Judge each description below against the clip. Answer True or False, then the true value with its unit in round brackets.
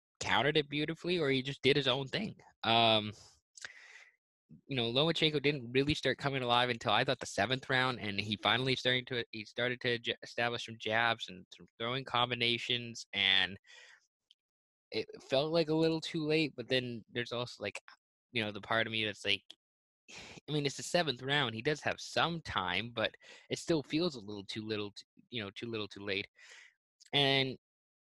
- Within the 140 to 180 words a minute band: False (190 wpm)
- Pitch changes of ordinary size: True (4.2 semitones)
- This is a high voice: False (125 Hz)